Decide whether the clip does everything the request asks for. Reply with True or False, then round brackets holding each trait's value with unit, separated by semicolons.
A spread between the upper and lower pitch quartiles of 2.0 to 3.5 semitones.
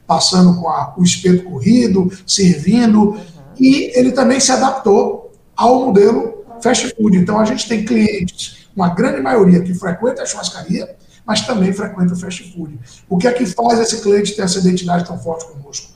False (4.8 semitones)